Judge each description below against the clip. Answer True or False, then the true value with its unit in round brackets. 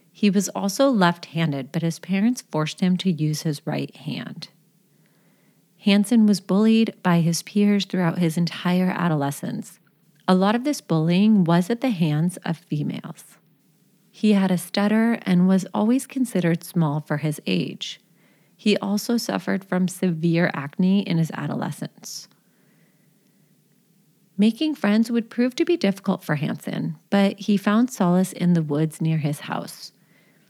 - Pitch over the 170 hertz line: True (185 Hz)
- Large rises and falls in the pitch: False (3.7 semitones)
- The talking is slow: False (150 wpm)